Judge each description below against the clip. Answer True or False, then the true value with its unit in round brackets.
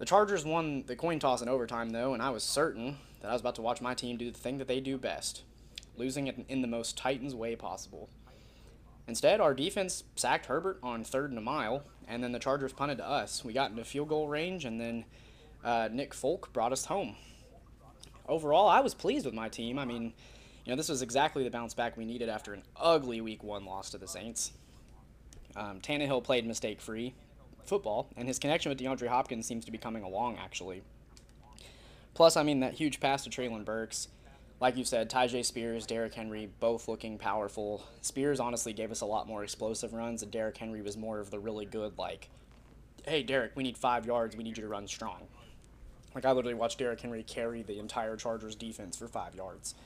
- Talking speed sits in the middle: False (210 wpm)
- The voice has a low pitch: True (120 Hz)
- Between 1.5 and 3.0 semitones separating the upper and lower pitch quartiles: True (2.6 semitones)